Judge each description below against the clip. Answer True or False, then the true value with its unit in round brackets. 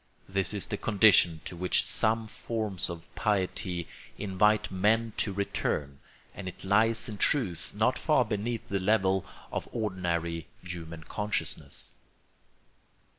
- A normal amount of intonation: True (3.3 semitones)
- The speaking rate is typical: False (125 wpm)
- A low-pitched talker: True (100 Hz)